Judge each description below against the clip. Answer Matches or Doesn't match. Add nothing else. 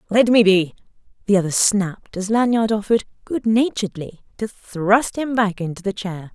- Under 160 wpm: Doesn't match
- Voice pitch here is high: Matches